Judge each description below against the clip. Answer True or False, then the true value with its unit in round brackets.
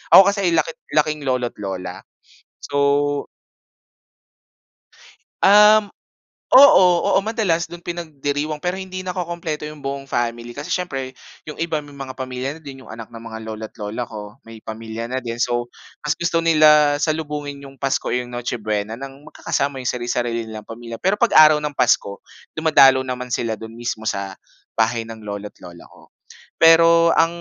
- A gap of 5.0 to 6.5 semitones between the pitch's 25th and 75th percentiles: True (5.3 semitones)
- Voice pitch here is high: False (135 Hz)